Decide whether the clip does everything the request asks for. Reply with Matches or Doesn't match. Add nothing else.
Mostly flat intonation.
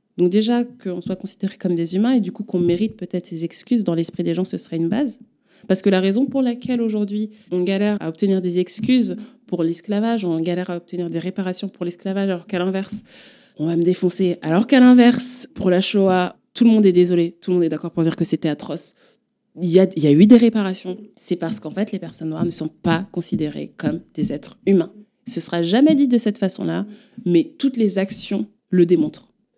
Doesn't match